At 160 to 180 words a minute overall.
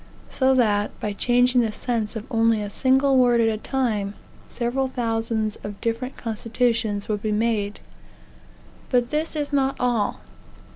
No: average, 150 wpm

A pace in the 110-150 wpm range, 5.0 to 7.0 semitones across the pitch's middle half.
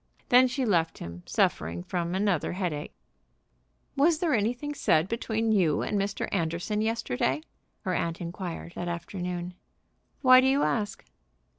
Yes: average, 140 wpm; wide, 5.4 semitones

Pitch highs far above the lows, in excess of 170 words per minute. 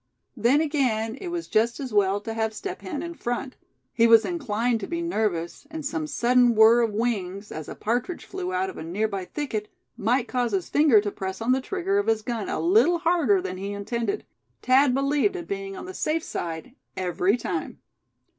Yes: wide, 6.6 semitones; average, 200 wpm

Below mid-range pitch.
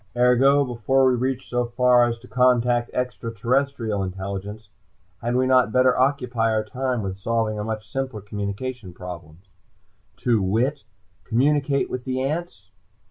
Yes: low, 120 Hz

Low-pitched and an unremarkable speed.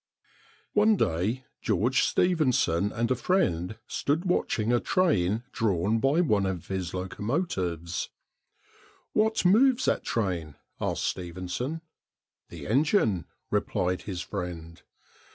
No: low, 105 Hz; slow, 110 wpm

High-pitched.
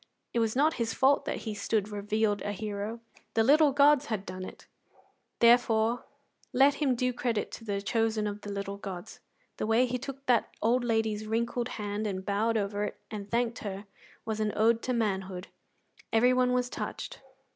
Yes: high, 225 Hz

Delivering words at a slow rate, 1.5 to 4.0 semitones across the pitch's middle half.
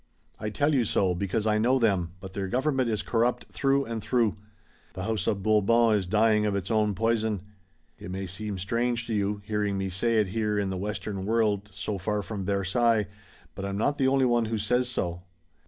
No: fast, 205 wpm; average, 2.9 semitones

